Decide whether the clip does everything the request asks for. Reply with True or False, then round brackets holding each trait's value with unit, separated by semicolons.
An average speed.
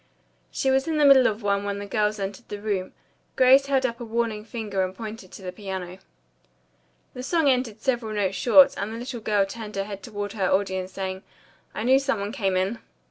False (215 wpm)